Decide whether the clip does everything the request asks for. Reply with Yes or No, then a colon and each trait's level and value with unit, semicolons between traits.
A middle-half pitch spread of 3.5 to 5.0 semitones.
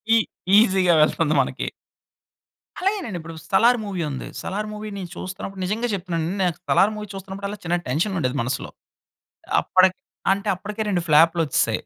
Yes: average, 4.0 semitones